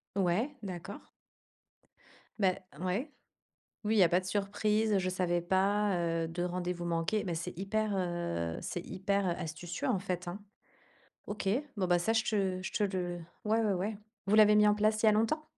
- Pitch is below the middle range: No, high, 190 Hz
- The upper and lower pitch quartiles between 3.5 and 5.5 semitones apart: No, average, 3.1 semitones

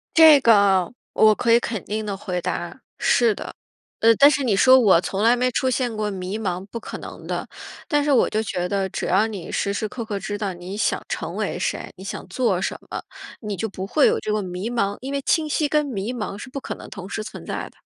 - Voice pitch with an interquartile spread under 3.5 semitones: No, average, 4.1 semitones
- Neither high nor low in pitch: No, high, 215 Hz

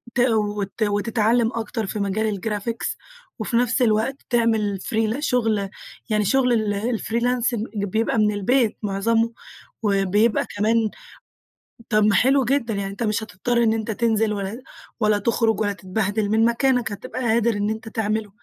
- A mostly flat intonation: Yes, narrow, 2.2 semitones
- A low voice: No, high, 220 Hz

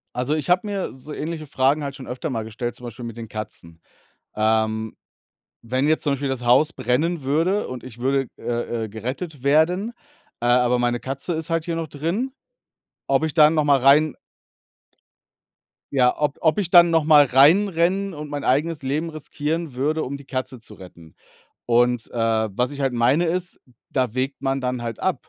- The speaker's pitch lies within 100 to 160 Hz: Yes, medium, 140 Hz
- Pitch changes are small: No, average, 4.4 semitones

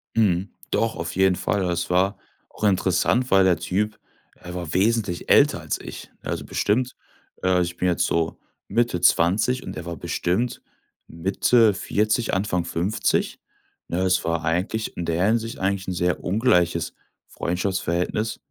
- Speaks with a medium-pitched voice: No, very low, 95 Hz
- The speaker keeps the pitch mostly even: No, average, 3.5 semitones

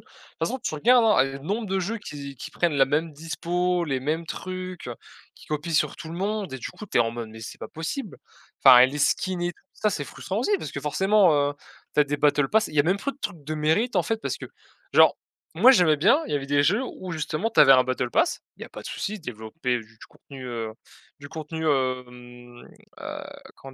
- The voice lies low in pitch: No, medium, 155 Hz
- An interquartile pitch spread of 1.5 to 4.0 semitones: No, wide, 5.6 semitones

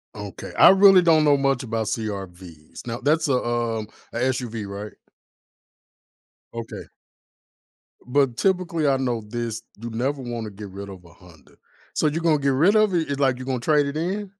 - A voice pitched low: Yes, low, 125 Hz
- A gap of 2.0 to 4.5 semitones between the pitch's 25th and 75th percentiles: No, wide, 5.4 semitones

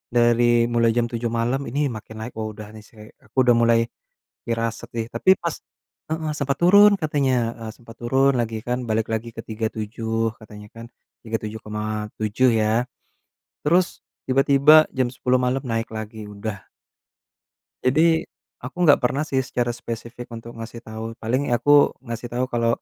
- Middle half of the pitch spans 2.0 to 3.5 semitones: Yes, average, 2.7 semitones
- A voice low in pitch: Yes, low, 115 Hz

